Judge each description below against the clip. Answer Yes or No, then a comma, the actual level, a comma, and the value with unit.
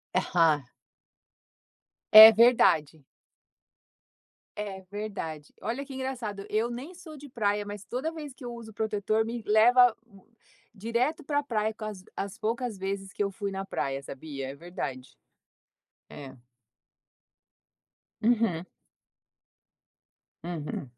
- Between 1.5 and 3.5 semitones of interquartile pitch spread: No, average, 4.6 semitones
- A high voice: Yes, high, 215 Hz